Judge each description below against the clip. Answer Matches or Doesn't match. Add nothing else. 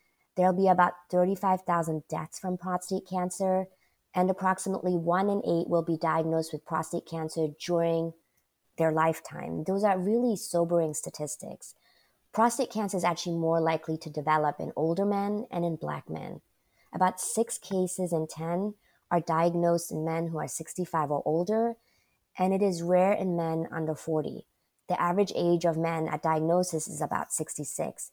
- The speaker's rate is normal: Matches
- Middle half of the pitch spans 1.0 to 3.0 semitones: Matches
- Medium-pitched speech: Matches